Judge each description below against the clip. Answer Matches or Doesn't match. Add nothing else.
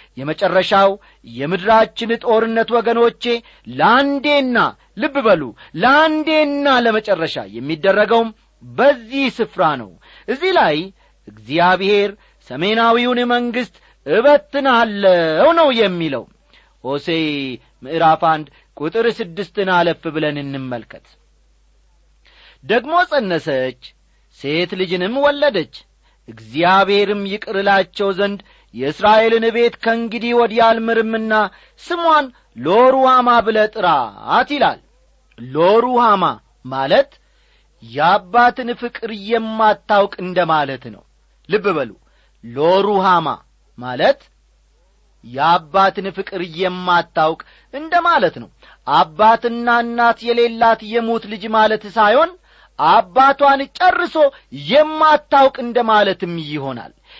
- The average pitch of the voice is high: Matches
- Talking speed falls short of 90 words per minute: Matches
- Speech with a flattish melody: Doesn't match